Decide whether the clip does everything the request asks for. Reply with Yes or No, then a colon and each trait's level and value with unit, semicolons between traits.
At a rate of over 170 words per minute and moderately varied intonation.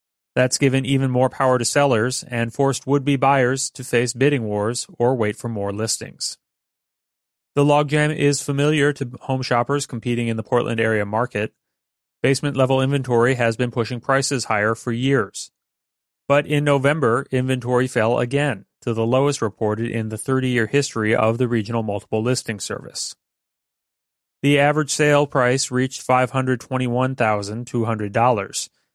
No: average, 145 wpm; average, 3.0 semitones